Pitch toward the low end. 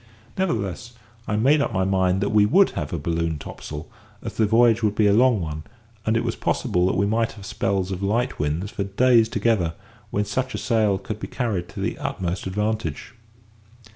Yes: low, 105 Hz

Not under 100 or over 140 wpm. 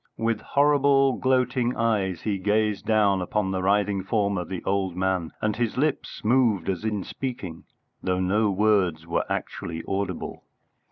No: average, 155 wpm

